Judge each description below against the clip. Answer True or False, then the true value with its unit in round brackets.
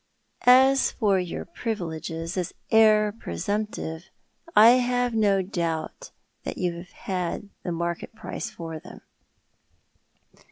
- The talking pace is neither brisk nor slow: False (110 wpm)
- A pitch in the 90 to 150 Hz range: False (195 Hz)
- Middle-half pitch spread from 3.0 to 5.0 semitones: True (4.7 semitones)